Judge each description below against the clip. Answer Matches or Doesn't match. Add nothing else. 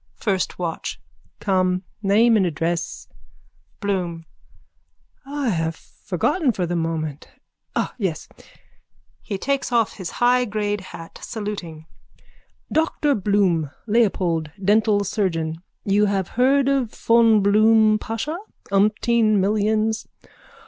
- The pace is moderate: Doesn't match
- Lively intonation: Doesn't match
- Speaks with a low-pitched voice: Doesn't match